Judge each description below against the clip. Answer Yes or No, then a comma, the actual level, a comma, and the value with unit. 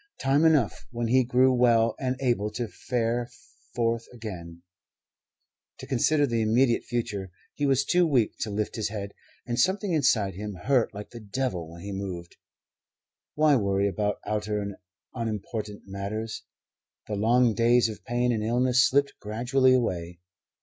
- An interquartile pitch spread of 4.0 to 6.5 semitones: No, average, 3.6 semitones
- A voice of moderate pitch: No, low, 115 Hz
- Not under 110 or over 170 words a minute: Yes, average, 155 wpm